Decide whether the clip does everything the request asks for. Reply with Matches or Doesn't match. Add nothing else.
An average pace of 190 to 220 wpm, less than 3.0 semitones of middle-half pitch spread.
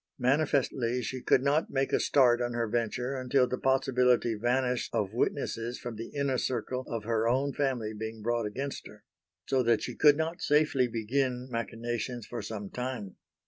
Doesn't match